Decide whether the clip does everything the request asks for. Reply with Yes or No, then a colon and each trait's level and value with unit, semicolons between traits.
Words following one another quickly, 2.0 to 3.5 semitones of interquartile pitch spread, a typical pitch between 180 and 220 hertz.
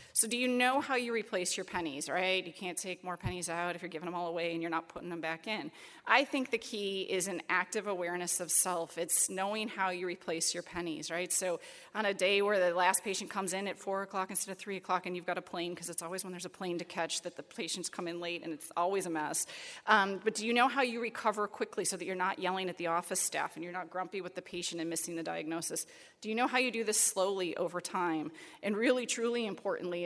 Yes: fast, 265 wpm; average, 2.7 semitones; medium, 185 Hz